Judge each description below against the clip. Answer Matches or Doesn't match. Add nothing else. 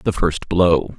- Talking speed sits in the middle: Matches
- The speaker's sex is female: Doesn't match